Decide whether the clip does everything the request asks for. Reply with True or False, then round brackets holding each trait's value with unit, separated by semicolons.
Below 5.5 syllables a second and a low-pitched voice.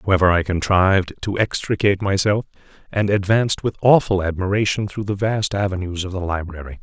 False (5.8 syllables/s; 95 Hz)